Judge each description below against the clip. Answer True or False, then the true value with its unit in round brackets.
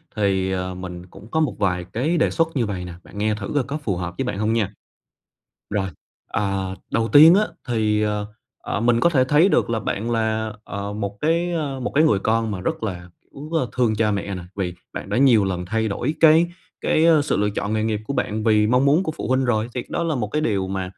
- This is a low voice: True (110 Hz)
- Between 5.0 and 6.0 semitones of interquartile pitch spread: True (5.5 semitones)